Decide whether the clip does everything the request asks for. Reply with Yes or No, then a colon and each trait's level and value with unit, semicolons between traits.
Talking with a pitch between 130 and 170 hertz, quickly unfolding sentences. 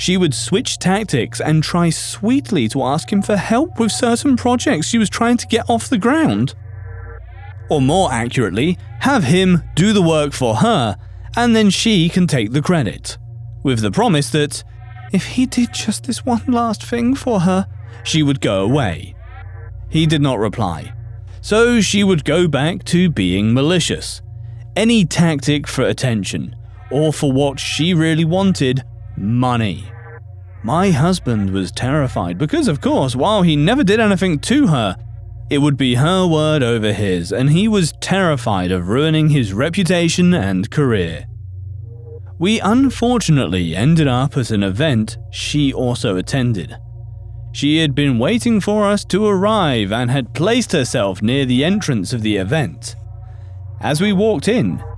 No: medium, 140 Hz; average, 155 wpm